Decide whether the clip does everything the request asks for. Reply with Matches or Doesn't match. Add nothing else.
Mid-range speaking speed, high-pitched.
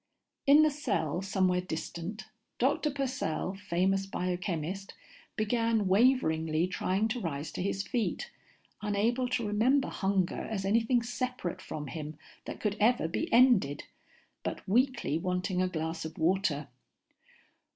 Doesn't match